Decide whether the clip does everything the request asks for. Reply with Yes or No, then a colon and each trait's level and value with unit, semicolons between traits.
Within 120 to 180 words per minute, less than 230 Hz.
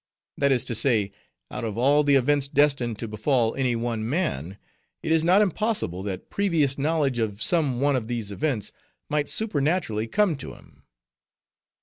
Yes: average, 165 wpm; low, 135 Hz